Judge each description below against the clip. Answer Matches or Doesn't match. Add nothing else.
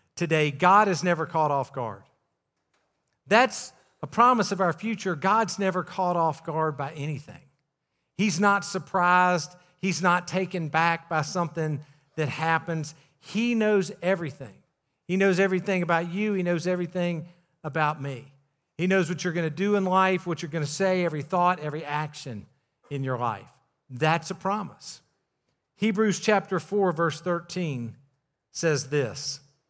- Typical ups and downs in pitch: Matches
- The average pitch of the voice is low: Doesn't match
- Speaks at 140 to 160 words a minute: Matches